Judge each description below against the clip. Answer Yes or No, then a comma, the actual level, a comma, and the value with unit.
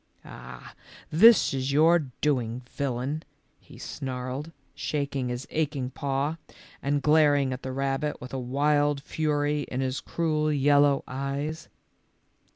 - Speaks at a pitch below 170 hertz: Yes, medium, 140 Hz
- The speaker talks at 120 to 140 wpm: Yes, slow, 135 wpm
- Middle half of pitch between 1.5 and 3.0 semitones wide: Yes, narrow, 2.4 semitones